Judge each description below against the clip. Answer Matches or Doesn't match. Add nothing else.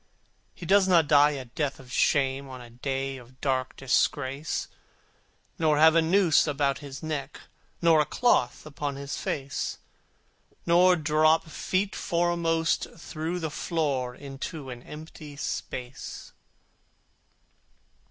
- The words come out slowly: Matches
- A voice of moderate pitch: Matches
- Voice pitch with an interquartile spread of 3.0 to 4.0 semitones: Matches